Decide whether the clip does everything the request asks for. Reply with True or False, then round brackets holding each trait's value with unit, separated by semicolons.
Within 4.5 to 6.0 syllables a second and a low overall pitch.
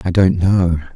False (4.0 syllables/s; 90 Hz)